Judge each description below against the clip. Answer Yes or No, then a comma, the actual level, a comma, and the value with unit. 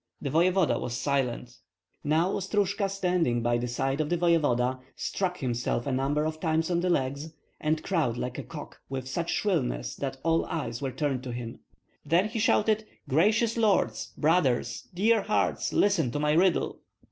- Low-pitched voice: No, medium, 155 Hz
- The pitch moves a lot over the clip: Yes, wide, 5.8 semitones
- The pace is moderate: Yes, average, 170 wpm